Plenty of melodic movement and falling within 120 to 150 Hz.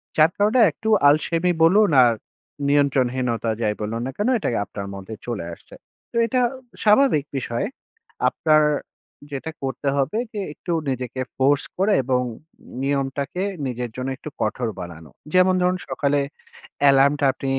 Yes: wide, 6.2 semitones; medium, 140 Hz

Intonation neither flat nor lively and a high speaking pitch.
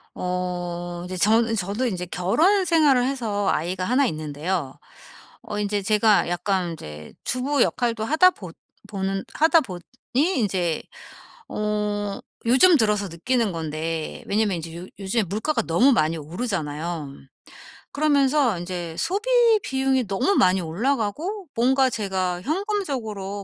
No: wide, 6.6 semitones; high, 205 Hz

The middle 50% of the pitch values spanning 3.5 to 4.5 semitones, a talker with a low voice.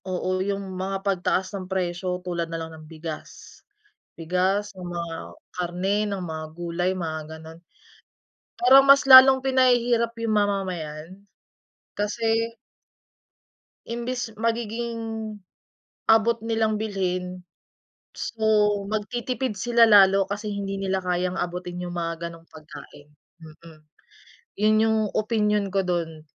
No: average, 4.0 semitones; high, 195 Hz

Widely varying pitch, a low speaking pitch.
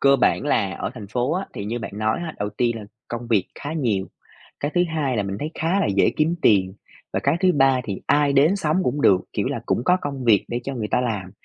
Yes: wide, 5.8 semitones; low, 125 Hz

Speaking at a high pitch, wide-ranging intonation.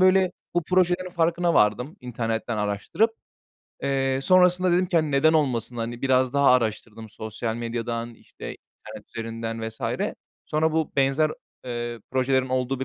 No: low, 130 Hz; wide, 5.7 semitones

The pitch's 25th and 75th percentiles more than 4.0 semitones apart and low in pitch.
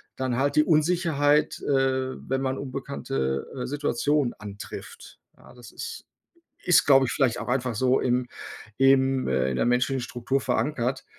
No: narrow, 2.5 semitones; low, 130 Hz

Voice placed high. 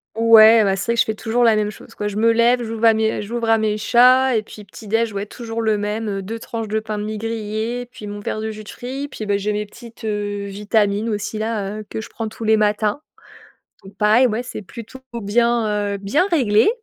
Yes: high, 220 Hz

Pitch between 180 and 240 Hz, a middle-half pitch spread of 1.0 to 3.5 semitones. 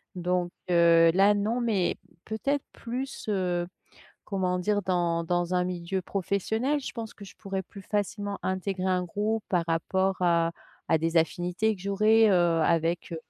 Yes: medium, 185 Hz; average, 3.1 semitones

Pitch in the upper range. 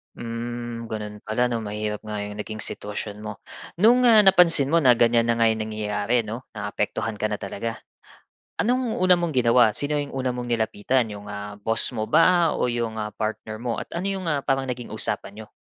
No: low, 115 Hz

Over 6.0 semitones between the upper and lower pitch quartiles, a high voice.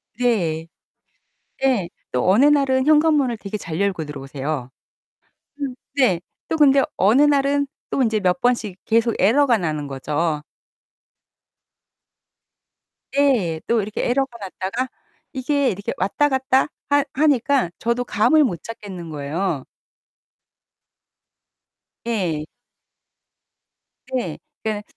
Yes: wide, 7.6 semitones; high, 225 Hz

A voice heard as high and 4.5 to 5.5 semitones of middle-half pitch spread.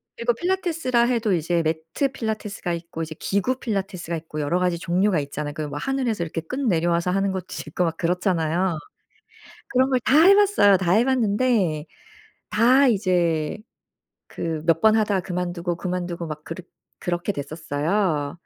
No: medium, 180 Hz; average, 5.1 semitones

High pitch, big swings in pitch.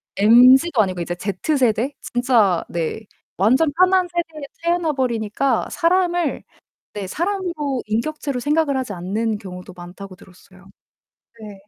Yes: high, 245 Hz; wide, 7.8 semitones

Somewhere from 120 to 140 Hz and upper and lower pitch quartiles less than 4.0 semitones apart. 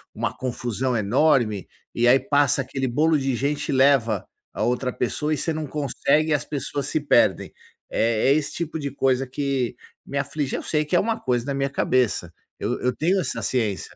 Yes: low, 135 Hz; average, 3.2 semitones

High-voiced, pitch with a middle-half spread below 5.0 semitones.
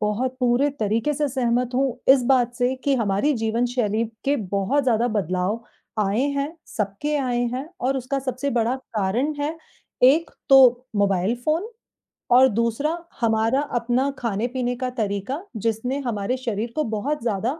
Yes: high, 245 Hz; average, 3.6 semitones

